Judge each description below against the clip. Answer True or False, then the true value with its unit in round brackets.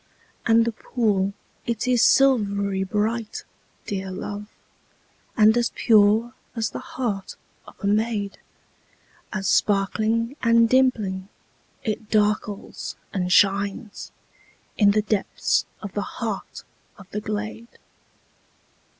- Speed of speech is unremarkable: False (110 wpm)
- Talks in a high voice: True (210 Hz)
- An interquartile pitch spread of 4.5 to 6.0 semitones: False (2.4 semitones)